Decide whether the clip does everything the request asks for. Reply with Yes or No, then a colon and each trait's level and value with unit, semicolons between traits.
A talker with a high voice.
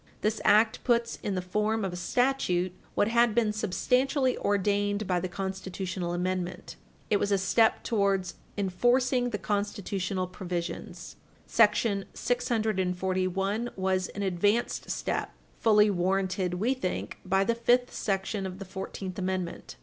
Yes: high, 195 Hz